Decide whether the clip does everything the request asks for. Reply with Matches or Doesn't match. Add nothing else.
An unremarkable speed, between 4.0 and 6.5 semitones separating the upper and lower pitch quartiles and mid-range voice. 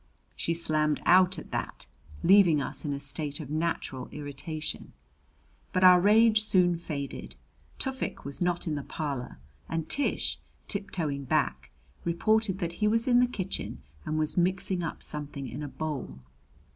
Matches